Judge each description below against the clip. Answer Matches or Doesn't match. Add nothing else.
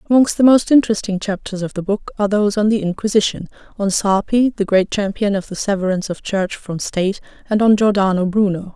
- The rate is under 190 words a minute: Doesn't match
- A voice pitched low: Doesn't match